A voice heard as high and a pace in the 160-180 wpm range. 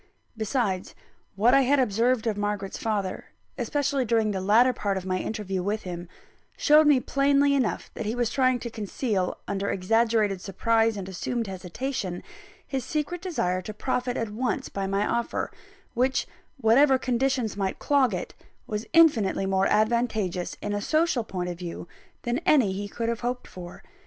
Yes: high, 225 Hz; average, 165 wpm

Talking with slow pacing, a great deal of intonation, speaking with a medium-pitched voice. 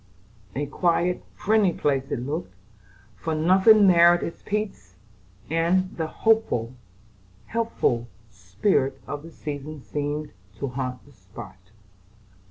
Yes: slow, 115 wpm; wide, 5.9 semitones; medium, 155 Hz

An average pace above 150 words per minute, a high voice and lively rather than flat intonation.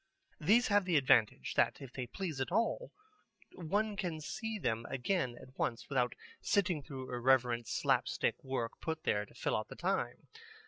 No: average, 170 wpm; medium, 140 Hz; wide, 7.5 semitones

